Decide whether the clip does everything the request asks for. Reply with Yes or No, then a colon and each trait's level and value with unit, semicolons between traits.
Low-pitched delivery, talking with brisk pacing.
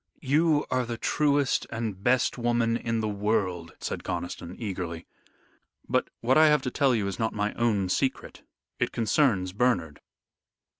No: low, 115 Hz; average, 155 wpm